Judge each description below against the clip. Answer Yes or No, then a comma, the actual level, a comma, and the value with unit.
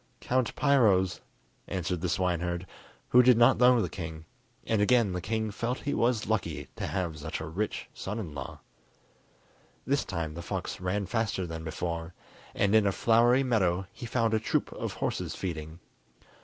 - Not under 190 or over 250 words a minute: No, average, 170 wpm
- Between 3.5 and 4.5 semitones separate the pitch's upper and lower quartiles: No, average, 5.0 semitones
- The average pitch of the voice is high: No, low, 100 Hz